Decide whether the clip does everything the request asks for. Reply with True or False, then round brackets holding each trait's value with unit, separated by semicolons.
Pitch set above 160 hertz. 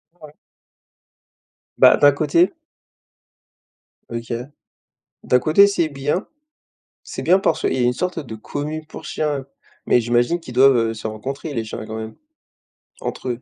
False (135 Hz)